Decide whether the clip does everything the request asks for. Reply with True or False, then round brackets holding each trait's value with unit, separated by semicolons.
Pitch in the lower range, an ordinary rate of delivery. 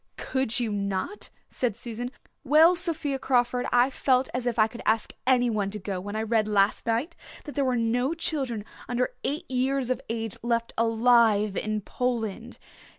False (240 Hz; 170 wpm)